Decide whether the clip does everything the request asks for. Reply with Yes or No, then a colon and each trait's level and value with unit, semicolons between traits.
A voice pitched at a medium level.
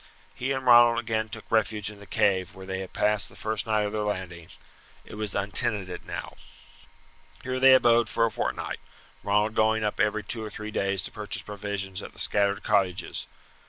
No: low, 105 Hz